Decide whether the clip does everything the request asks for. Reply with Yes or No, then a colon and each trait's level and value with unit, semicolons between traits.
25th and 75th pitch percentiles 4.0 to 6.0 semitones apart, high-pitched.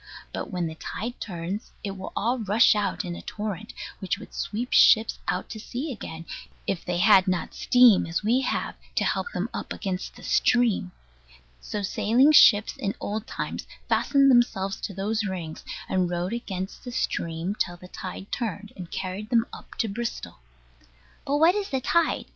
Yes: average, 4.3 semitones; high, 205 Hz